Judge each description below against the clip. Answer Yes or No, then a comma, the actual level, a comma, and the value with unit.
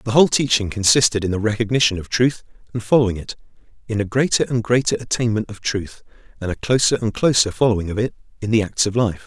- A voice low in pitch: Yes, low, 110 Hz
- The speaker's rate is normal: No, fast, 215 wpm